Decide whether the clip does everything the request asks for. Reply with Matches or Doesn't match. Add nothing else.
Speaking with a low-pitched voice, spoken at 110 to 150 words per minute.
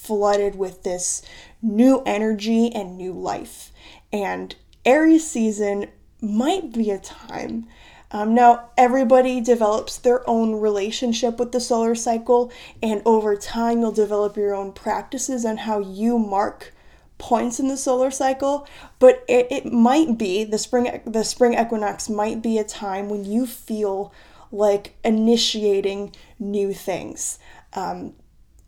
Doesn't match